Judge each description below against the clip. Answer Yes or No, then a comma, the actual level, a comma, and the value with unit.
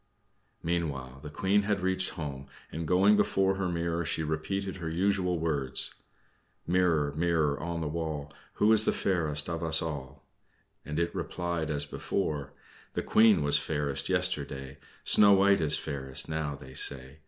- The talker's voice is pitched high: No, very low, 80 Hz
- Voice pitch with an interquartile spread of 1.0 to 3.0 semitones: No, average, 3.9 semitones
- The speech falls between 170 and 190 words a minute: No, average, 155 wpm